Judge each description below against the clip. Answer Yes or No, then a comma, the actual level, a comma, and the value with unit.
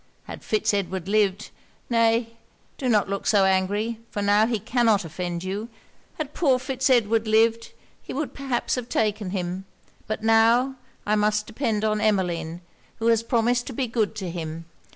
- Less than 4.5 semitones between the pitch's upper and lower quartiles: Yes, average, 3.0 semitones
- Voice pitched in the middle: No, high, 215 Hz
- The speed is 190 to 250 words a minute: No, average, 170 wpm